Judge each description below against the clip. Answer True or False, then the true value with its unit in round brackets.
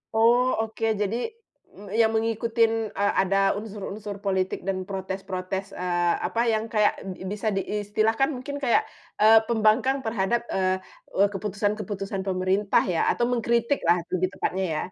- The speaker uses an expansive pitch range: False (2.8 semitones)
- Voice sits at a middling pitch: False (205 Hz)